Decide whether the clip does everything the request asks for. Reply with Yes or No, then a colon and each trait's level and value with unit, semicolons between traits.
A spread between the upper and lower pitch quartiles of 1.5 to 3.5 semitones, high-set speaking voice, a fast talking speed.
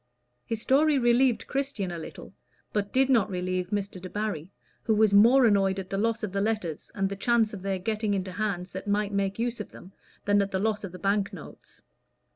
Yes: narrow, 2.6 semitones; high, 205 Hz; fast, 215 wpm